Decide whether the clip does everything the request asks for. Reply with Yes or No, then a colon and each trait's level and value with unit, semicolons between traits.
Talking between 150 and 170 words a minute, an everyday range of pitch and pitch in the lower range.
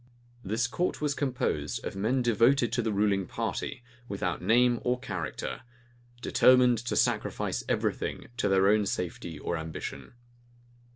No: average, 140 wpm; average, 4.4 semitones; low, 115 Hz